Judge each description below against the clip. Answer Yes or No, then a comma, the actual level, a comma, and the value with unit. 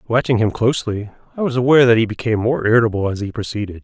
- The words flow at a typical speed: No, fast, 220 wpm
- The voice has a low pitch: Yes, low, 115 Hz